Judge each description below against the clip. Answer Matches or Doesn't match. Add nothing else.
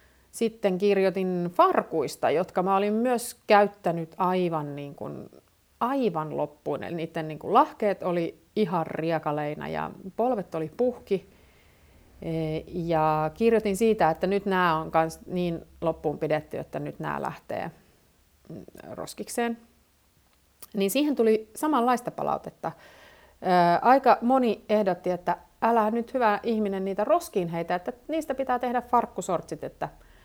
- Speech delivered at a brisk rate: Doesn't match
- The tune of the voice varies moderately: Doesn't match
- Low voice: Doesn't match